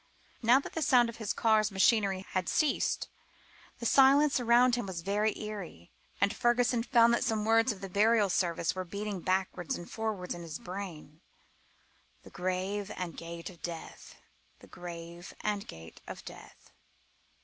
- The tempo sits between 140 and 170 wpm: Yes, average, 160 wpm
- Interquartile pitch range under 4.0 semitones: No, average, 4.4 semitones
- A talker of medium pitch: No, high, 200 Hz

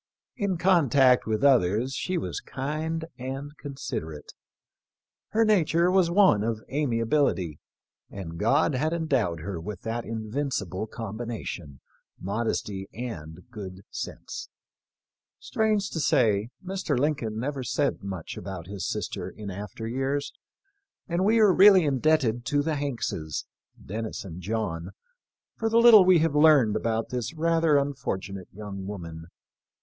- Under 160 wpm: Yes, average, 140 wpm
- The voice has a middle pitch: No, low, 125 Hz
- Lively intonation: Yes, wide, 7.5 semitones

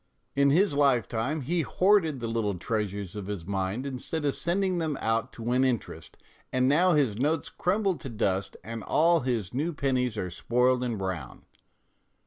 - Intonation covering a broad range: Yes, wide, 6.0 semitones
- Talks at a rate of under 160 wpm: No, average, 170 wpm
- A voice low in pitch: Yes, low, 125 Hz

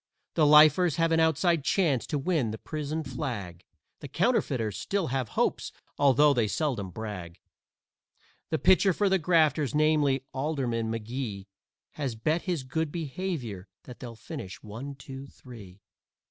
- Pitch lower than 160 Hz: Yes, medium, 140 Hz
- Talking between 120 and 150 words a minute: Yes, average, 145 wpm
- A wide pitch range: Yes, wide, 5.7 semitones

